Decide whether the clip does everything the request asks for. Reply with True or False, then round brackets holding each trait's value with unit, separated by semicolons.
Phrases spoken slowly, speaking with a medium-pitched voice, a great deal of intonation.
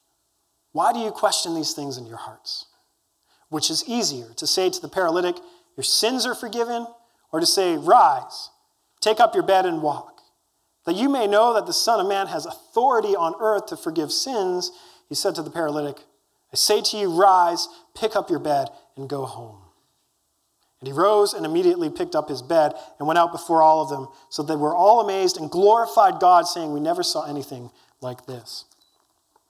False (195 wpm; 180 Hz; 7.2 semitones)